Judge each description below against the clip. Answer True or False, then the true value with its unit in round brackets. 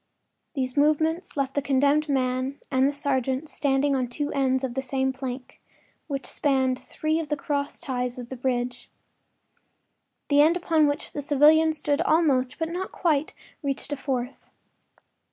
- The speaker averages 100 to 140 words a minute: False (165 wpm)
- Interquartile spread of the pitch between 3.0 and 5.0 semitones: False (2.4 semitones)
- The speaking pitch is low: False (280 Hz)